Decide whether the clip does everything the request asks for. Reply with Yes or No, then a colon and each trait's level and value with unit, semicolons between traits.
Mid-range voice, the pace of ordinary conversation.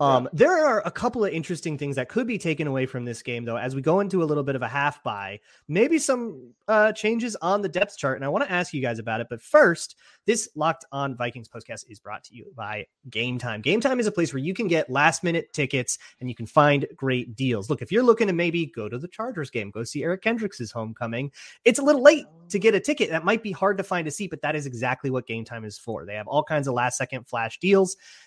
No: medium, 150 Hz; fast, 270 wpm